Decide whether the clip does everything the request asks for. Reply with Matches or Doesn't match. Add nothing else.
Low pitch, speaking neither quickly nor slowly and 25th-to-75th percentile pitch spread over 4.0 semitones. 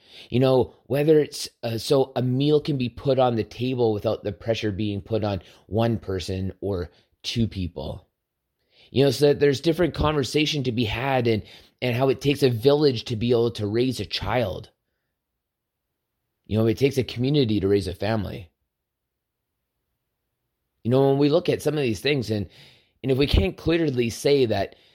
Matches